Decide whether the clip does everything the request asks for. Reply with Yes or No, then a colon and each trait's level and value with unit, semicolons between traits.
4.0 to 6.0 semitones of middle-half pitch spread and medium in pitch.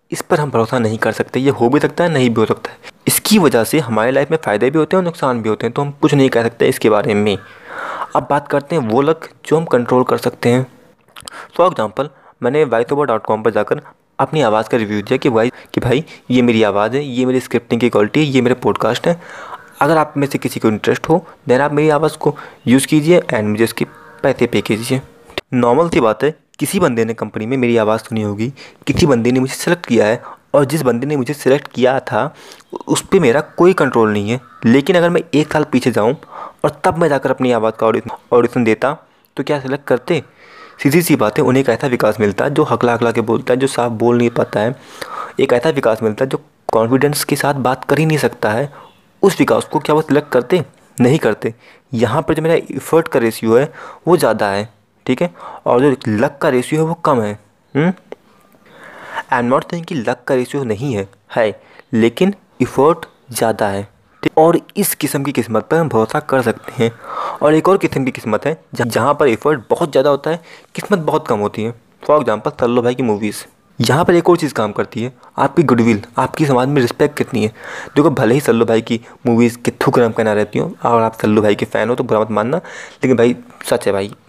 No: average, 4.6 semitones; low, 130 Hz